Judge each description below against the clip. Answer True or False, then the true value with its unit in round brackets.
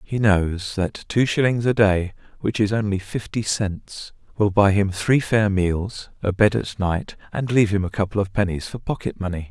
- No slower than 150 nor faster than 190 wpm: False (200 wpm)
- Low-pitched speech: True (100 Hz)